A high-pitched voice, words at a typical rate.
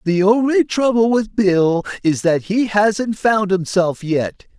Yes: high, 200 Hz; average, 155 wpm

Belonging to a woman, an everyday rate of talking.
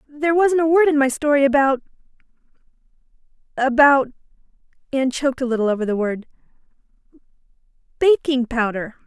No: female; slow, 105 wpm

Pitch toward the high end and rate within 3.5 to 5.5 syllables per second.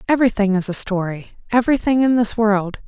No: high, 215 Hz; 6.0 syllables/s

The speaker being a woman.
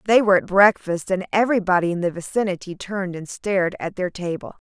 Yes: female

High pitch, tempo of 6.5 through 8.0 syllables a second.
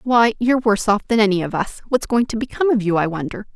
Yes: high, 220 Hz; 6.7 syllables/s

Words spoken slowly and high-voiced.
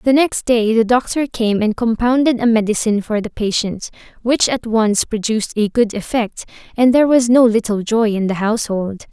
No: average, 190 wpm; high, 225 Hz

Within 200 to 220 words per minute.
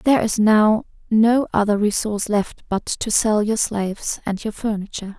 No: average, 175 wpm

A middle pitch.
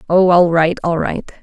Yes: medium, 170 Hz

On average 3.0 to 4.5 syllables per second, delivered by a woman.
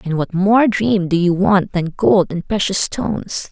Yes: 4.1 syllables/s; female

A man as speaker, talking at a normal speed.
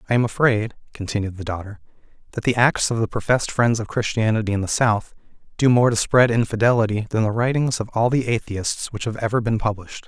No: male; fast, 210 wpm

